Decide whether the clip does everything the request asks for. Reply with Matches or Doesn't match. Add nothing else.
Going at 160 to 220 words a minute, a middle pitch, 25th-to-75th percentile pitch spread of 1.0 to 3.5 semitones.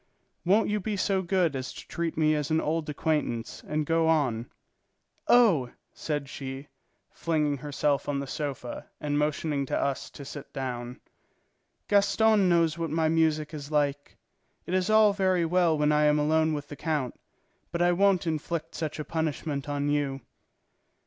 Matches